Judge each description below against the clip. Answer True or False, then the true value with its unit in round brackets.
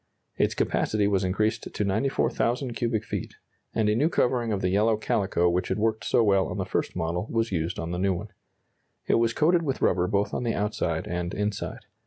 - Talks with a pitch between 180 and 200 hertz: False (105 Hz)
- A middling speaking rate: False (210 wpm)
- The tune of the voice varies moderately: True (3.8 semitones)